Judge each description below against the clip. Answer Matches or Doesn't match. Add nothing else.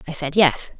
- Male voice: Doesn't match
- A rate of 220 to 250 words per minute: Matches